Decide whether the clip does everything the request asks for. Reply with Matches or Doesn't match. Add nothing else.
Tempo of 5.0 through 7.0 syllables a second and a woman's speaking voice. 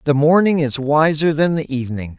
Doesn't match